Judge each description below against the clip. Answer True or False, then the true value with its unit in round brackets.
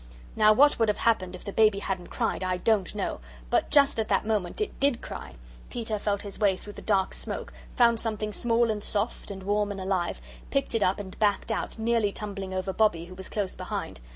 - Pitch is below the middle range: False (210 Hz)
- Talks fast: True (220 wpm)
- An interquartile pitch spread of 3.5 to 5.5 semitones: False (2.7 semitones)